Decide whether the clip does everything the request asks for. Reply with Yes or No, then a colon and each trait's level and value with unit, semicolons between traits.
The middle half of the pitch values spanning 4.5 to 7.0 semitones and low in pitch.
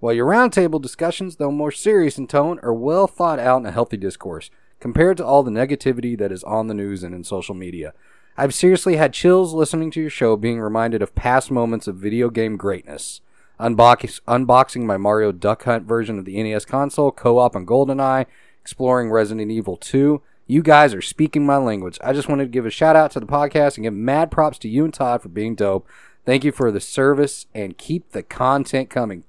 Yes: average, 4.8 semitones; low, 130 Hz